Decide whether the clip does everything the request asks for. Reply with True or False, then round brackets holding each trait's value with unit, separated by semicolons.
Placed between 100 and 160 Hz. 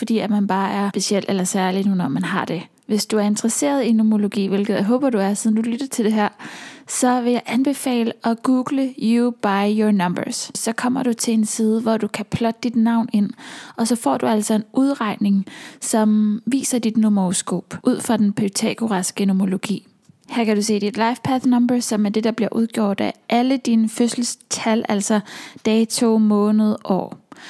False (225 Hz)